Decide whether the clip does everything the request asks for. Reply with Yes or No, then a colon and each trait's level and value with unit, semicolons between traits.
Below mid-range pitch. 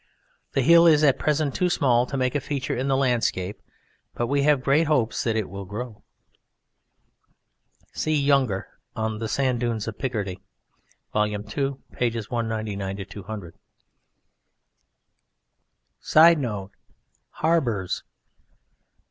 Yes: low, 120 Hz